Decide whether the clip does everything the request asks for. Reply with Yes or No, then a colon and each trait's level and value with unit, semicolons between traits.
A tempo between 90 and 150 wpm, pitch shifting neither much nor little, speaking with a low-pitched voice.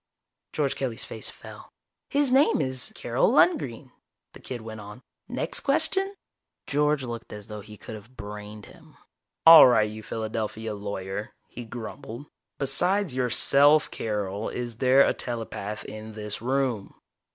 Yes: average, 140 wpm; average, 4.5 semitones; low, 115 Hz